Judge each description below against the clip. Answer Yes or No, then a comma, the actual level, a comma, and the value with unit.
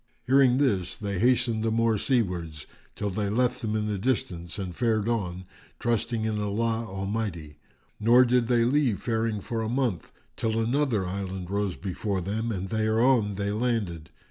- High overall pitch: No, low, 110 Hz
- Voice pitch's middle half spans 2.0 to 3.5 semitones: Yes, average, 3.2 semitones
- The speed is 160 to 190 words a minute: Yes, average, 165 wpm